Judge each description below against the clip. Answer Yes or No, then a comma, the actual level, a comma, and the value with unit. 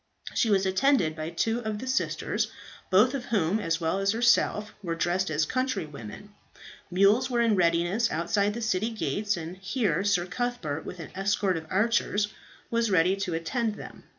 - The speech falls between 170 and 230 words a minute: Yes, average, 175 wpm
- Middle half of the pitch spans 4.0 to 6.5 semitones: Yes, average, 4.6 semitones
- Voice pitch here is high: Yes, high, 200 Hz